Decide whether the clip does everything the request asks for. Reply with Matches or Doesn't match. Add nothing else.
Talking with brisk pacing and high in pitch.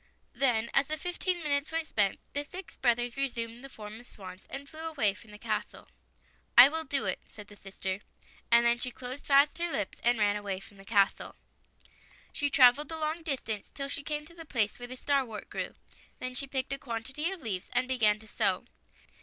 Matches